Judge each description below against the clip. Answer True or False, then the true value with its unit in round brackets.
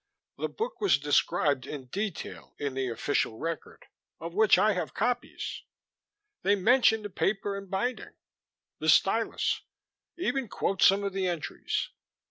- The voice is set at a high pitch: True (195 Hz)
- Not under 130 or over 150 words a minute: True (140 wpm)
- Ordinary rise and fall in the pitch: False (5.9 semitones)